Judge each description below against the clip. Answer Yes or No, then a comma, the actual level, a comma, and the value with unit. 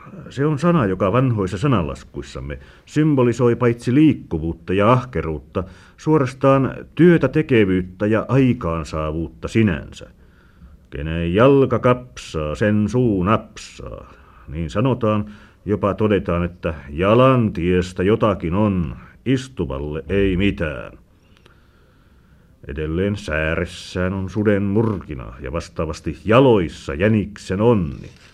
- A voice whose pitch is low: Yes, low, 100 Hz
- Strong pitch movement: Yes, wide, 6.2 semitones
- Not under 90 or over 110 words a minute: Yes, slow, 95 wpm